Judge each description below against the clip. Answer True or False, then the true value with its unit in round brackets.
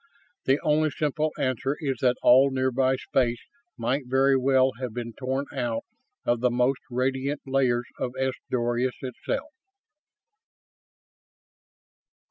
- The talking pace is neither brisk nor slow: False (120 wpm)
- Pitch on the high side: False (130 Hz)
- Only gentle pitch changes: True (1.6 semitones)